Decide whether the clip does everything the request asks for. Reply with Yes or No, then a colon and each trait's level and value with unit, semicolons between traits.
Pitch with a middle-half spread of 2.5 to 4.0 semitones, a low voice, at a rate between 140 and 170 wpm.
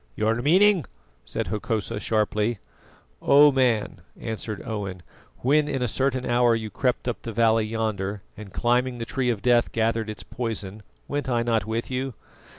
Yes: average, 2.8 semitones; low, 115 Hz; average, 160 wpm